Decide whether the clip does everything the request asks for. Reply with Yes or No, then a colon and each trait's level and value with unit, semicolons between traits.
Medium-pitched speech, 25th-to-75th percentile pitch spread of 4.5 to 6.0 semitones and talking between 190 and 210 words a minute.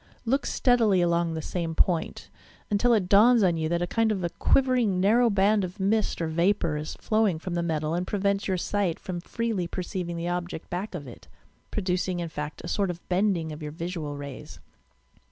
No: medium, 180 Hz; average, 3.4 semitones; fast, 205 wpm